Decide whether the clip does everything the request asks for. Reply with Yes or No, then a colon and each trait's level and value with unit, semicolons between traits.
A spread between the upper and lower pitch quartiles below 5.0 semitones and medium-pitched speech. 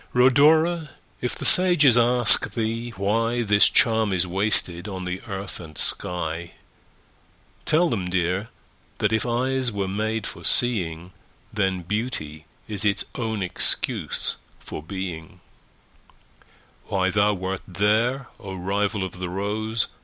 No: average, 4.0 semitones; low, 105 Hz